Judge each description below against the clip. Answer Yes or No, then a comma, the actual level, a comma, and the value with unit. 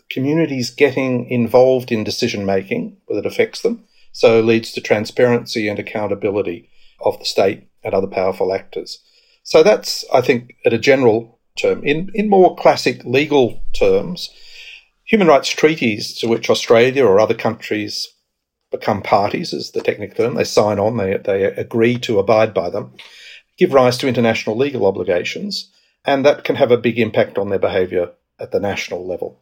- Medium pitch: Yes, medium, 180 Hz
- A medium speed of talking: Yes, average, 165 wpm